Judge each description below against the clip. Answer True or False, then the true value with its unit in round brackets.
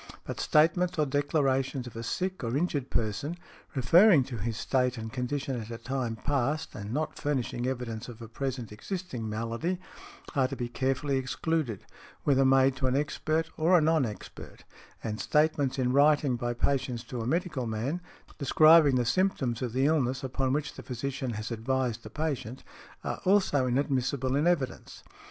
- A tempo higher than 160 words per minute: True (170 wpm)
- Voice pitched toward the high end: False (130 Hz)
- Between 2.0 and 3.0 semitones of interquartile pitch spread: False (3.7 semitones)